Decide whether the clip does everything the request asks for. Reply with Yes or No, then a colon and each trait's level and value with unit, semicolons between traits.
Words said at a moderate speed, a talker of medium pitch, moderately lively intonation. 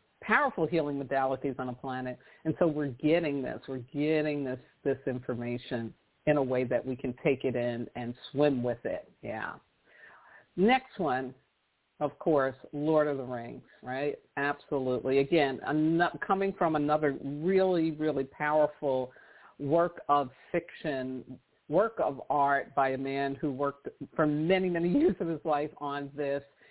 Yes: average, 150 wpm; medium, 145 Hz; average, 3.0 semitones